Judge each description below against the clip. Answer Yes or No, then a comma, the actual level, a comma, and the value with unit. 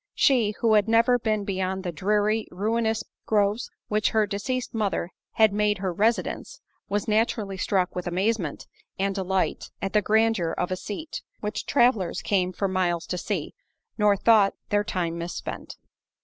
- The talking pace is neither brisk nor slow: Yes, average, 160 wpm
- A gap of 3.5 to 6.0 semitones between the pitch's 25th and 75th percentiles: No, average, 2.8 semitones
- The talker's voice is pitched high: Yes, high, 205 Hz